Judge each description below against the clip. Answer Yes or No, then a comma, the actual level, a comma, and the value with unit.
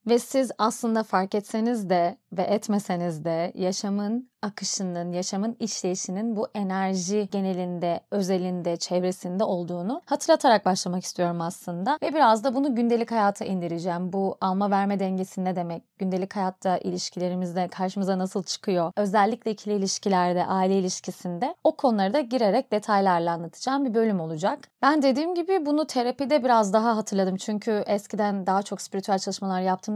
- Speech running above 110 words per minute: Yes, fast, 140 wpm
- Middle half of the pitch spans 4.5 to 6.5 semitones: No, average, 3.5 semitones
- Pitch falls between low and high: No, high, 200 Hz